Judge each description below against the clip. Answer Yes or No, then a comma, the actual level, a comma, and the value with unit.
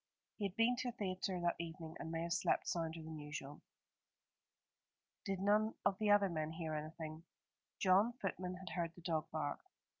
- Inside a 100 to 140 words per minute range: No, average, 180 wpm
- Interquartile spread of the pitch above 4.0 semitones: No, average, 3.6 semitones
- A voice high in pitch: No, medium, 170 Hz